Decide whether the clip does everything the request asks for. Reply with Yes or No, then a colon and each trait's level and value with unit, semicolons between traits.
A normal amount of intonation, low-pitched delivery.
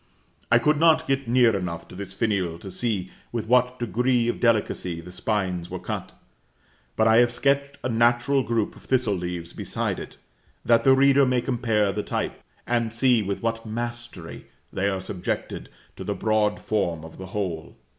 Yes: average, 4.3 semitones; low, 115 Hz